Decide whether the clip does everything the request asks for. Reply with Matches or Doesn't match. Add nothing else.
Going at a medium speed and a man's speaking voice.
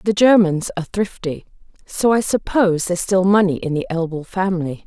Doesn't match